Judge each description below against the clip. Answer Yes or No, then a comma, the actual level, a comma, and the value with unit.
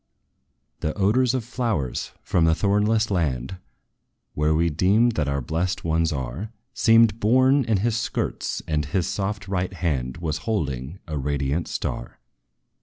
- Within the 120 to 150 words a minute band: Yes, average, 145 wpm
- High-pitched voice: No, very low, 90 Hz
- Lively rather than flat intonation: Yes, wide, 6.2 semitones